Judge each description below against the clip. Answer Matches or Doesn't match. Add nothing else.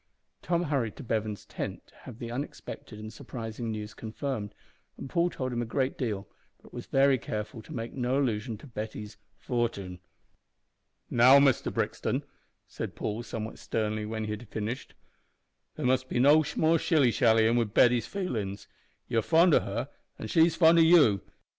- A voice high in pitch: Doesn't match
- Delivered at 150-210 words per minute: Matches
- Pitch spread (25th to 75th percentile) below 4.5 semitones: Matches